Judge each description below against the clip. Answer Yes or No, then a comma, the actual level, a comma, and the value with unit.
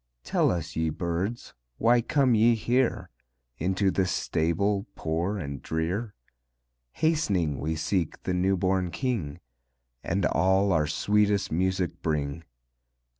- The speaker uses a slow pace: Yes, slow, 125 wpm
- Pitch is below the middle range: Yes, very low, 95 Hz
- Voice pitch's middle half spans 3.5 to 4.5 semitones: Yes, average, 4.1 semitones